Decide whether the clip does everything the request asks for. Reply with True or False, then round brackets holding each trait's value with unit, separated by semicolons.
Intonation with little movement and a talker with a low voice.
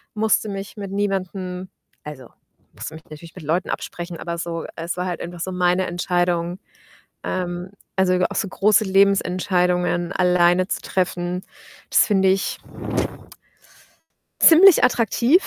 False (1.9 semitones; 180 Hz)